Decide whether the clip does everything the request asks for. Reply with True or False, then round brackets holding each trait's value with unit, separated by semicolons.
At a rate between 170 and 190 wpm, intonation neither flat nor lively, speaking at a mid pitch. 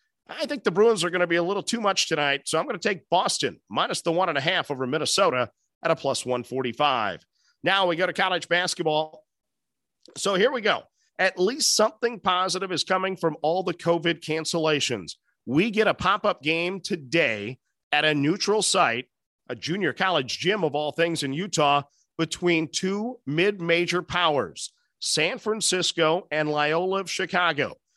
True (175 wpm; 3.9 semitones; 175 Hz)